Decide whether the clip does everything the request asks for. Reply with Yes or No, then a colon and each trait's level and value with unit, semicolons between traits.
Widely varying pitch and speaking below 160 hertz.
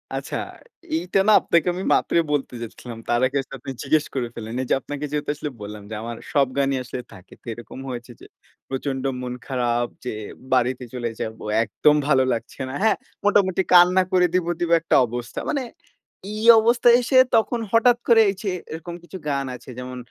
Yes: wide, 6.8 semitones; medium, 140 Hz